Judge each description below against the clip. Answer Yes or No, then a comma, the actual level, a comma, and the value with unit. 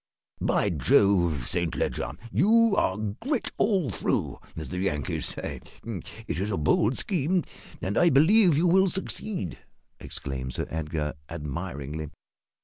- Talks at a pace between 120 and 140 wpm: Yes, slow, 135 wpm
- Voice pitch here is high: No, low, 100 Hz